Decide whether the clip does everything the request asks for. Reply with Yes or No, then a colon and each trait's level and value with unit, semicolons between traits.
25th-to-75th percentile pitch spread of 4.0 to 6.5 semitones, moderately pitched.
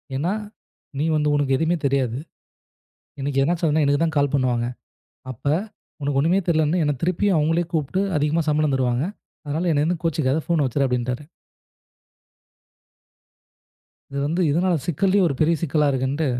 No: average, 3.2 semitones; medium, 150 Hz